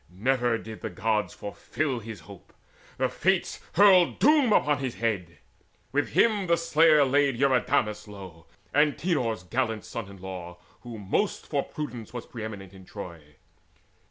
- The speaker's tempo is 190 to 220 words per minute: No, average, 150 wpm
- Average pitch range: No, wide, 6.4 semitones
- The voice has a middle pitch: No, low, 115 Hz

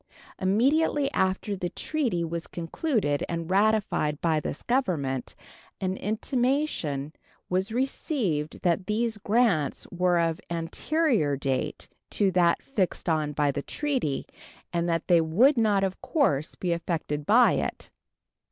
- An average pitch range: No, wide, 6.4 semitones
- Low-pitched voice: No, medium, 185 Hz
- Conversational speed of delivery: No, slow, 130 wpm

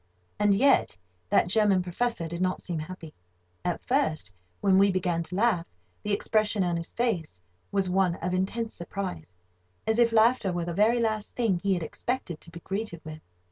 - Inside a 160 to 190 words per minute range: Yes, average, 180 wpm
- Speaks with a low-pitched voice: No, high, 190 Hz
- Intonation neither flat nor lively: Yes, average, 4.1 semitones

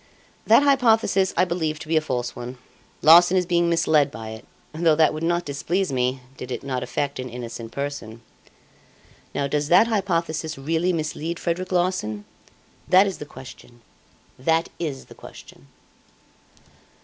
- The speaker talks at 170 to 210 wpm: No, average, 155 wpm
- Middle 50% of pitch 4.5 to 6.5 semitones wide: Yes, average, 5.1 semitones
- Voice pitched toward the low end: No, medium, 155 Hz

